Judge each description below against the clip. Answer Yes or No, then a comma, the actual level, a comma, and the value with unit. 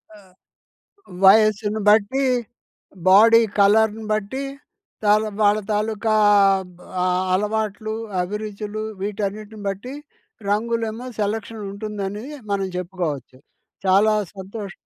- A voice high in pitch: Yes, high, 210 Hz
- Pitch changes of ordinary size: No, narrow, 1.6 semitones